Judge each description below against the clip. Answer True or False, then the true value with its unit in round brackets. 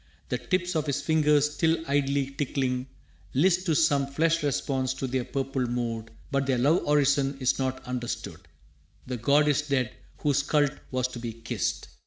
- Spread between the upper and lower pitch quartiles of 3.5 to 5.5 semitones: False (2.5 semitones)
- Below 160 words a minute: False (170 wpm)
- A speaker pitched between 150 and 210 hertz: False (140 Hz)